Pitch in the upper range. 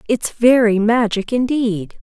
Yes: high, 230 Hz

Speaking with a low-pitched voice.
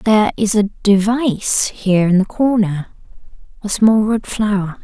No: high, 205 Hz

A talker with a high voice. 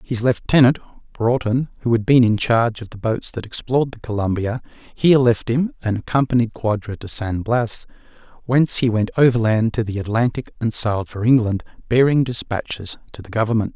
No: low, 115 Hz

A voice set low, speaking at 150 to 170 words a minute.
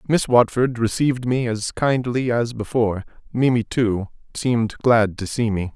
Yes: low, 120 Hz; average, 155 wpm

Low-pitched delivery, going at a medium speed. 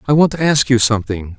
No: low, 120 Hz; fast, 260 wpm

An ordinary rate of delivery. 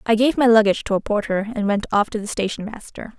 No: fast, 265 wpm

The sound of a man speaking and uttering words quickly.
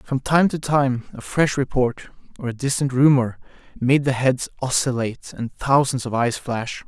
No: male; average, 175 wpm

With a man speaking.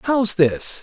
Yes: male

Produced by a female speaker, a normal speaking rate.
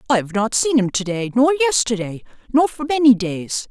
No: female; fast, 210 wpm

